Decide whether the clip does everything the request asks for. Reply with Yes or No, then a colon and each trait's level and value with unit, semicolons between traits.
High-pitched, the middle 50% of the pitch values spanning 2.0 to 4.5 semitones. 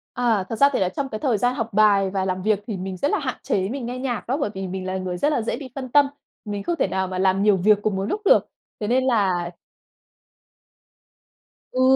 No: high, 210 Hz; average, 4.9 semitones